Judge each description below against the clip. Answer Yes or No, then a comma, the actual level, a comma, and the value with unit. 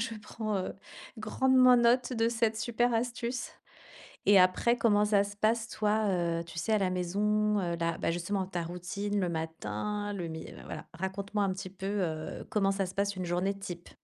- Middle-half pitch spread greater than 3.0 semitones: Yes, average, 3.5 semitones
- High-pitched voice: Yes, high, 200 Hz